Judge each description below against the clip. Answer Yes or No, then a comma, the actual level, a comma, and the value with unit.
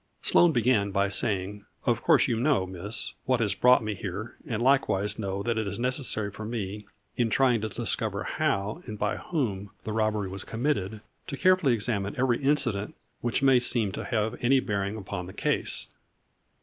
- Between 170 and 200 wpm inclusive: Yes, average, 185 wpm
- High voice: No, low, 110 Hz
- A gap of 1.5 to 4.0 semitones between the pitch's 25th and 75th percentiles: Yes, average, 3.7 semitones